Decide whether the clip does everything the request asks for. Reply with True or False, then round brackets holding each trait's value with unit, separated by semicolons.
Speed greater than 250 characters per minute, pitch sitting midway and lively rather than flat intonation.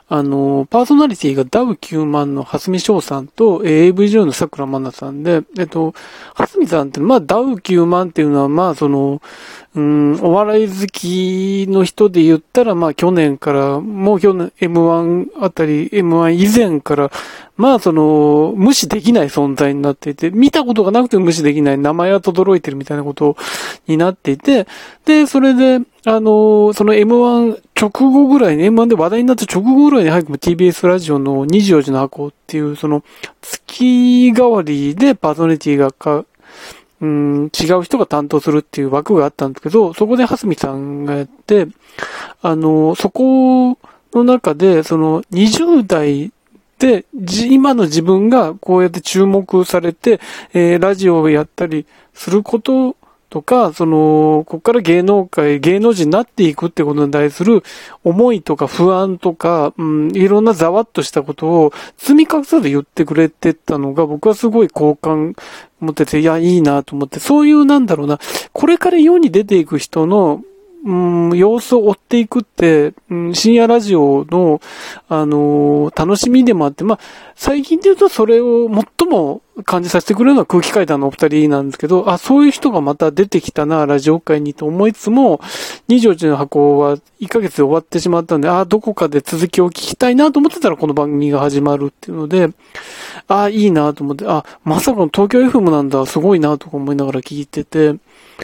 True (340 characters per minute; 175 Hz; 6.7 semitones)